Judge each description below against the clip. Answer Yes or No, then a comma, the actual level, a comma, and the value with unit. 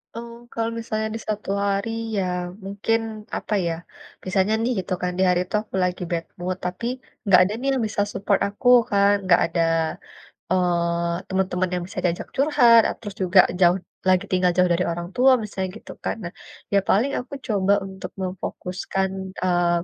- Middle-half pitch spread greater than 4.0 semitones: No, average, 2.9 semitones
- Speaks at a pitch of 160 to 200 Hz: Yes, high, 190 Hz